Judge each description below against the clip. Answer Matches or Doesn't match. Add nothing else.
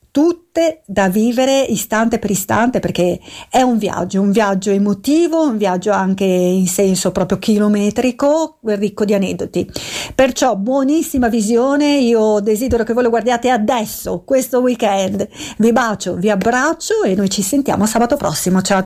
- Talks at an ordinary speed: Matches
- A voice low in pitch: Doesn't match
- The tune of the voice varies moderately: Matches